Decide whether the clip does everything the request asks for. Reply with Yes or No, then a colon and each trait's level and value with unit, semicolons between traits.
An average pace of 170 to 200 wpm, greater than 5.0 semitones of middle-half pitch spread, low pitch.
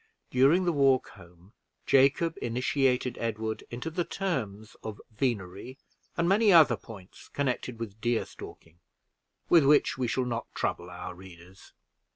No: average, 140 wpm; wide, 5.6 semitones; low, 125 Hz